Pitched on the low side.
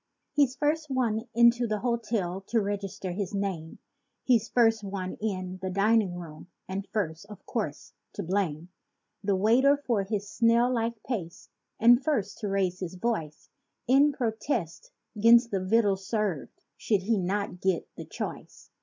No: high, 205 Hz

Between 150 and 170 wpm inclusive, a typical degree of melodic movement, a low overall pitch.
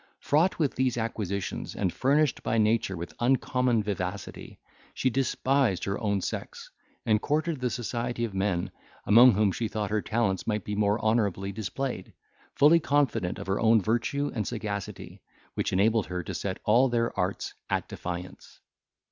Yes: average, 160 wpm; average, 4.1 semitones; low, 110 Hz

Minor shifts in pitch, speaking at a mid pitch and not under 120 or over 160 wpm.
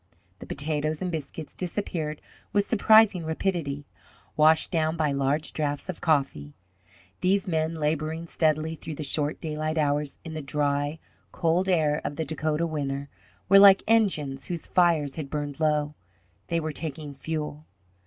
Yes: narrow, 2.3 semitones; medium, 155 Hz; average, 150 wpm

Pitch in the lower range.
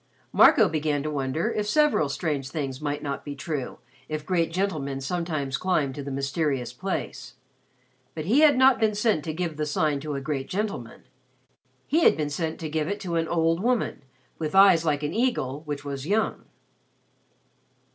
No: medium, 155 Hz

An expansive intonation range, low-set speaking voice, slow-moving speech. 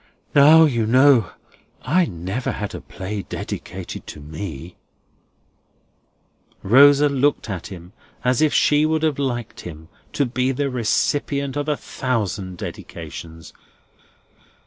Yes: wide, 7.1 semitones; low, 125 Hz; slow, 125 wpm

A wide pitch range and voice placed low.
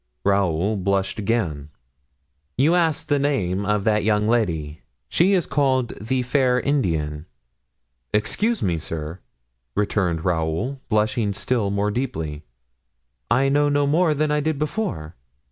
Yes: wide, 7.8 semitones; low, 110 Hz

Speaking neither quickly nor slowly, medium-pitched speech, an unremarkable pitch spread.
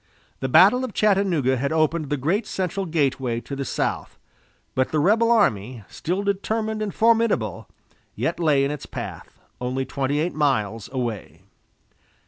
No: average, 150 wpm; medium, 150 Hz; wide, 7.4 semitones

